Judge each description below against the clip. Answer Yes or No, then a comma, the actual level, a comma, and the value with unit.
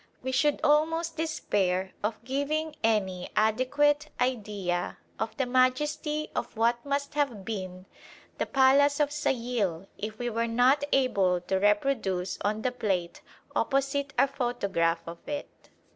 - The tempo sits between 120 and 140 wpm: Yes, slow, 135 wpm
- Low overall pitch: No, high, 245 Hz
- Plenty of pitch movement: Yes, wide, 5.9 semitones